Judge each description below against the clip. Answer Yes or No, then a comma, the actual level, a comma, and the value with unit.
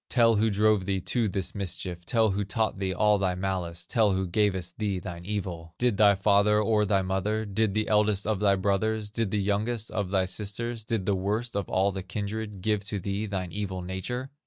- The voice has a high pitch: No, low, 100 Hz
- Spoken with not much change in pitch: Yes, narrow, 2.2 semitones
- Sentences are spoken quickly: Yes, fast, 210 wpm